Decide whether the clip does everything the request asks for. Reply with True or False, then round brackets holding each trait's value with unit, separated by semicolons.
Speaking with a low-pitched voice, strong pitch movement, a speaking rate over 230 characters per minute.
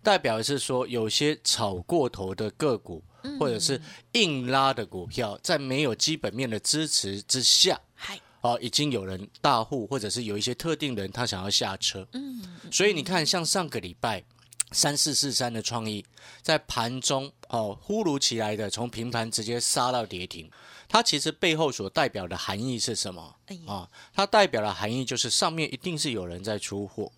True (125 Hz; 5.7 semitones; 265 characters per minute)